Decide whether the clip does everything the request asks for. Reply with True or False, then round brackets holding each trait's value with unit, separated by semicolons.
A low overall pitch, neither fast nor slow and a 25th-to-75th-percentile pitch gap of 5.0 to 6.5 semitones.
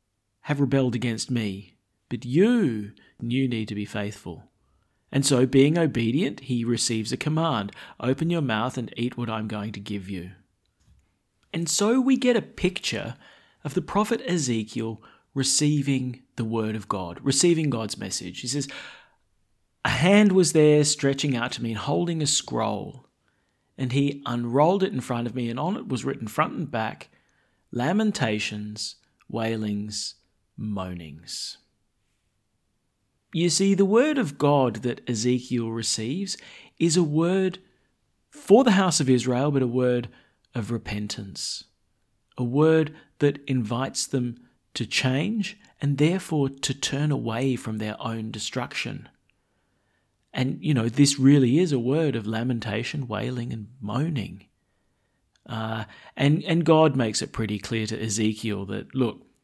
True (125 Hz; 145 wpm; 5.3 semitones)